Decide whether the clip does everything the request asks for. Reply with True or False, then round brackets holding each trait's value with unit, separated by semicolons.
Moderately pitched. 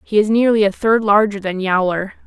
False (205 Hz)